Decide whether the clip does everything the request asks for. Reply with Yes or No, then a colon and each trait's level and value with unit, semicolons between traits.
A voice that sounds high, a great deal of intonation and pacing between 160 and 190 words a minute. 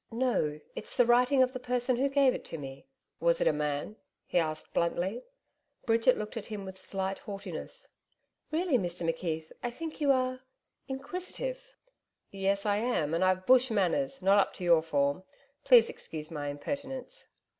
Yes: high, 220 Hz; wide, 7.2 semitones; average, 170 wpm